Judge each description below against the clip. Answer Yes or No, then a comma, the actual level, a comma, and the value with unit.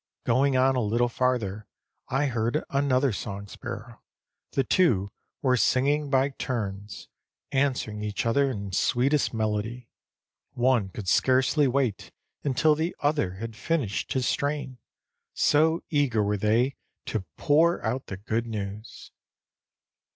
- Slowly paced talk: Yes, slow, 130 wpm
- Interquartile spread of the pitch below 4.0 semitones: No, average, 4.5 semitones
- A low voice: Yes, low, 125 Hz